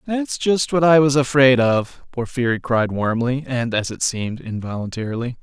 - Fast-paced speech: No, average, 165 wpm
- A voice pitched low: Yes, low, 130 Hz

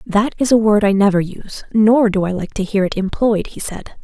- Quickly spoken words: Yes, fast, 255 wpm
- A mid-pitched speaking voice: No, high, 205 Hz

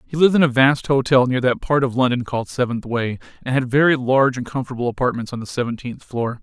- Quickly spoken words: Yes, fast, 235 wpm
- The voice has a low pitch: Yes, low, 130 Hz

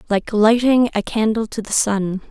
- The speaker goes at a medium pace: Yes, average, 180 wpm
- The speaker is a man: No, female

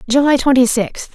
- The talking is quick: No, average, 155 wpm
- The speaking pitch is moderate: No, very high, 255 Hz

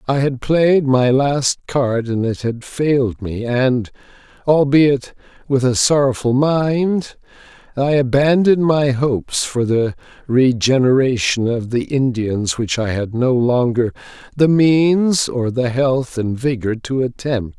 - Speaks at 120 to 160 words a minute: Yes, average, 140 wpm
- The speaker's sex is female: No, male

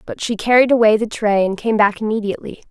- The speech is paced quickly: Yes, fast, 220 wpm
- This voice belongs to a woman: Yes, female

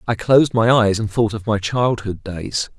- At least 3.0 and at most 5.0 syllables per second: Yes, 4.6 syllables/s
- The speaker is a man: Yes, male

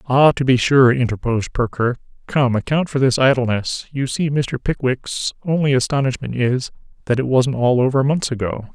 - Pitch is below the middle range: Yes, low, 130 Hz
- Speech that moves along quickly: No, average, 170 wpm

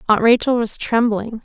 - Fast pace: No, average, 165 wpm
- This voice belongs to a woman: Yes, female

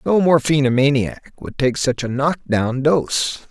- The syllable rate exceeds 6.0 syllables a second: No, 3.9 syllables/s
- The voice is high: No, low, 135 Hz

